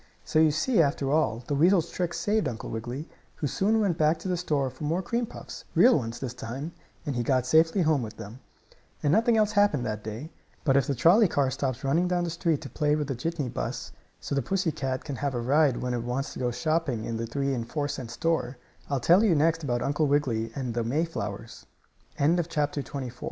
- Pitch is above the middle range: No, medium, 145 Hz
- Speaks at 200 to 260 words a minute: Yes, fast, 205 wpm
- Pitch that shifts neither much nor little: Yes, average, 5.0 semitones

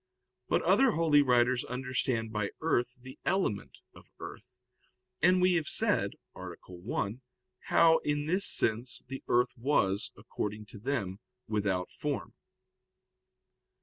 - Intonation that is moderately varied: No, wide, 5.7 semitones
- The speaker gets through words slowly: Yes, slow, 125 wpm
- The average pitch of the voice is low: Yes, low, 125 Hz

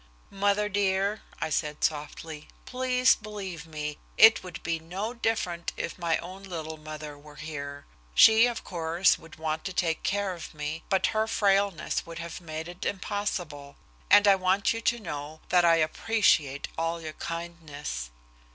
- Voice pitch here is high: No, medium, 170 Hz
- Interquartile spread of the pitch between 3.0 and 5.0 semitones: Yes, average, 4.4 semitones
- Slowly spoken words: No, average, 160 wpm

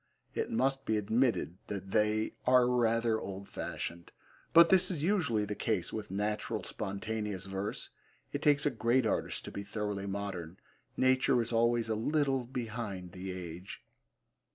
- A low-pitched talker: Yes, low, 110 Hz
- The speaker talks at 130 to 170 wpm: Yes, average, 155 wpm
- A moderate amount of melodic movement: Yes, average, 4.0 semitones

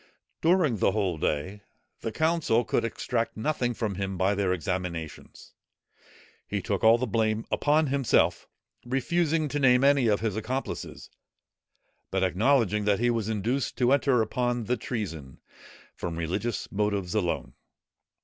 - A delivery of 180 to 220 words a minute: No, average, 140 wpm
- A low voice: Yes, low, 110 Hz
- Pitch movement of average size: Yes, average, 4.8 semitones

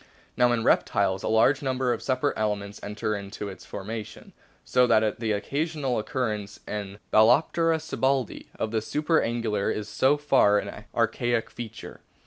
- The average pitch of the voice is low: Yes, low, 115 Hz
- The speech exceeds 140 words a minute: Yes, average, 150 wpm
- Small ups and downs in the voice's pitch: No, average, 4.0 semitones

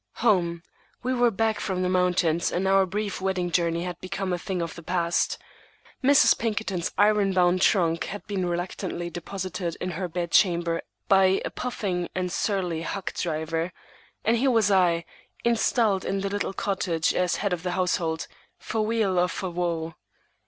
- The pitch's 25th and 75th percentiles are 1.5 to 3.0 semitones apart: Yes, narrow, 2.5 semitones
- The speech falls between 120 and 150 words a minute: No, average, 170 wpm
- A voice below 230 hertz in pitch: Yes, medium, 185 Hz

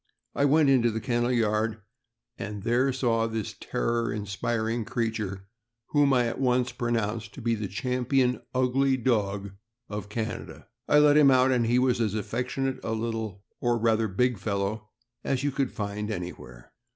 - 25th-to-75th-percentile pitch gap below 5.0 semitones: Yes, average, 3.1 semitones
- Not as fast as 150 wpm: No, average, 165 wpm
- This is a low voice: Yes, low, 115 Hz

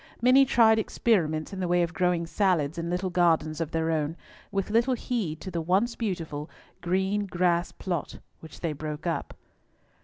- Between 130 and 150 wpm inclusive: No, average, 175 wpm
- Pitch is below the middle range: No, medium, 175 Hz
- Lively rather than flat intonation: No, average, 3.5 semitones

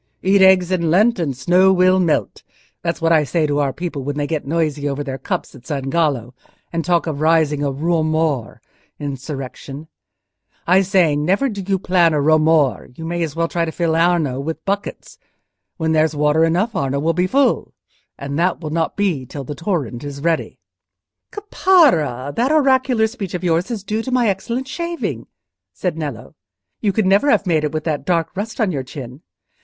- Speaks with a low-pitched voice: No, medium, 165 Hz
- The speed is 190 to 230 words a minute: Yes, average, 195 wpm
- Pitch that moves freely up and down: No, average, 4.5 semitones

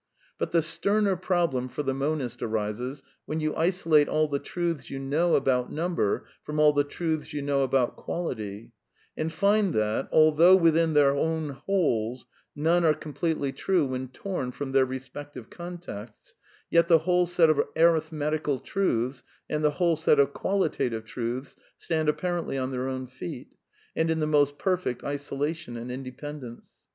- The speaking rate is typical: Yes, average, 160 wpm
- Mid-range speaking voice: Yes, medium, 150 Hz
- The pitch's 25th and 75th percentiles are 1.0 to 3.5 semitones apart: No, average, 4.1 semitones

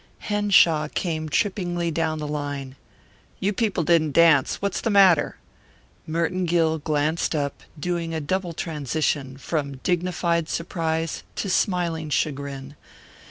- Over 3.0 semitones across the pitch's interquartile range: No, average, 2.7 semitones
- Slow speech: Yes, slow, 120 wpm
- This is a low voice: No, medium, 165 Hz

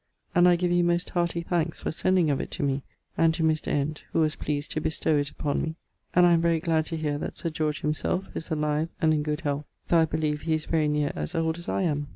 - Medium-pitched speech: Yes, medium, 160 Hz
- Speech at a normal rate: No, fast, 270 wpm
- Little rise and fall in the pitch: Yes, narrow, 2.1 semitones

